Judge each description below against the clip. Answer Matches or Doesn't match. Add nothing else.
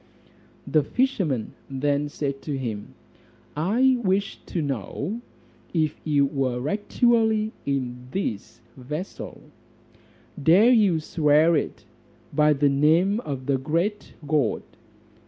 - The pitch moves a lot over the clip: Matches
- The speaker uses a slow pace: Matches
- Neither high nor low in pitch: Matches